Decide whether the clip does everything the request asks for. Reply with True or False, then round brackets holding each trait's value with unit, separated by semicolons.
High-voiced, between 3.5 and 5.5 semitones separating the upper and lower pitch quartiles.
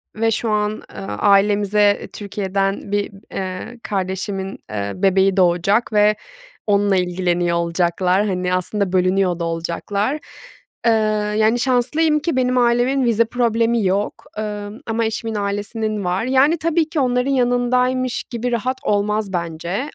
True (210 Hz; 4.2 semitones)